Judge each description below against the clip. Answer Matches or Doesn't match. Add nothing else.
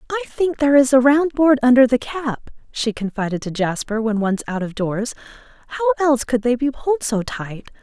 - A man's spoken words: Doesn't match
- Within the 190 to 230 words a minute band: Matches